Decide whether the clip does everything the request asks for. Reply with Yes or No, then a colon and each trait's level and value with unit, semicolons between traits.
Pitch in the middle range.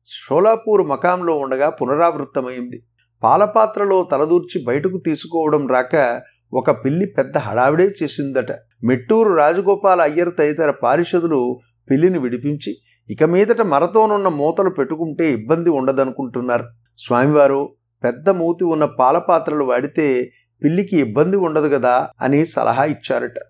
Yes: medium, 150 Hz